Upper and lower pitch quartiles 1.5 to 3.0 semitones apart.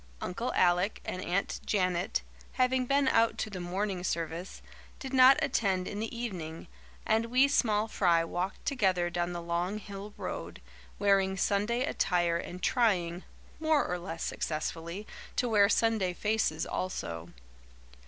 No: average, 4.2 semitones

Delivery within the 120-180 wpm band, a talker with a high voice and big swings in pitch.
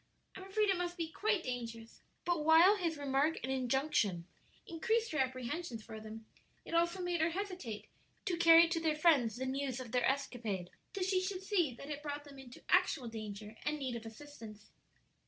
No: average, 190 wpm; very high, 290 Hz; wide, 6.1 semitones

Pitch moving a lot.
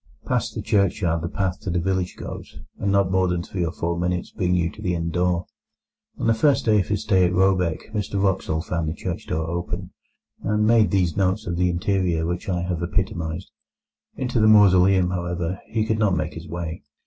No: narrow, 2.4 semitones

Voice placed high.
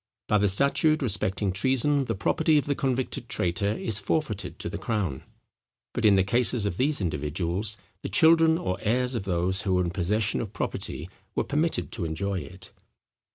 No: low, 105 Hz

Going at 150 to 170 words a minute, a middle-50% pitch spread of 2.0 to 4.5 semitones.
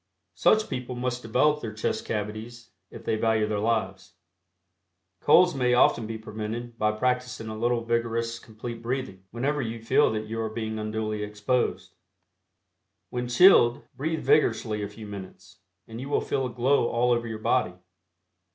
Yes: average, 160 wpm; narrow, 2.4 semitones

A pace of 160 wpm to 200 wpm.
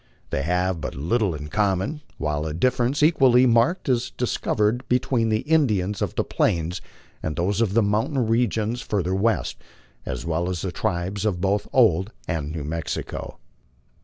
Yes: average, 170 wpm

